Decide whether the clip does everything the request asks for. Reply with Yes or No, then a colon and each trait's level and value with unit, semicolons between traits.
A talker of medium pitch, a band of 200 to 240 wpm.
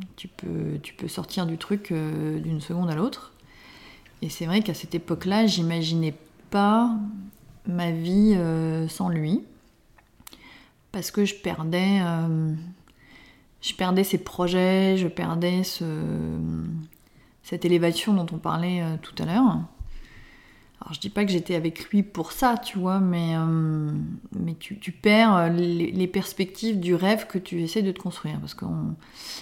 No: medium, 175 Hz; average, 155 wpm